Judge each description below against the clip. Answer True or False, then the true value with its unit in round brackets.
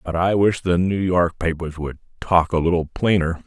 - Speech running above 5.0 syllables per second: False (4.8 syllables/s)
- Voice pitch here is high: False (85 Hz)